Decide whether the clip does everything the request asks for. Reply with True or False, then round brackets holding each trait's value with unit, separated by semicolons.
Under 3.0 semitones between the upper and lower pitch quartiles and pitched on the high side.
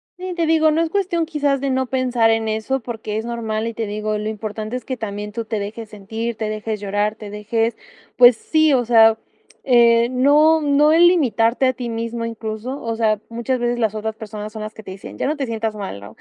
False (3.3 semitones; 230 Hz)